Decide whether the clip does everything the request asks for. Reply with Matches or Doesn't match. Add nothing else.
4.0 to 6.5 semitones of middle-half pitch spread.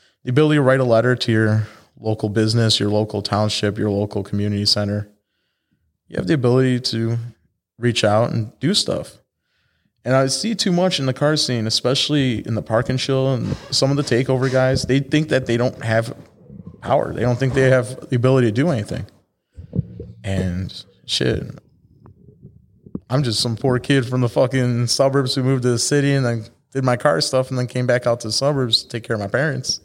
Doesn't match